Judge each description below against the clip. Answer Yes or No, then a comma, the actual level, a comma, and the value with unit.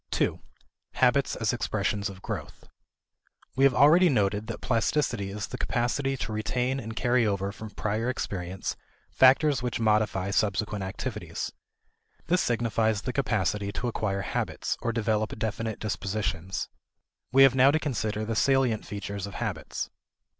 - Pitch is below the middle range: Yes, low, 110 Hz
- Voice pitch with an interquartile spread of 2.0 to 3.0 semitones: No, average, 3.7 semitones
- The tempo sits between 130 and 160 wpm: Yes, average, 145 wpm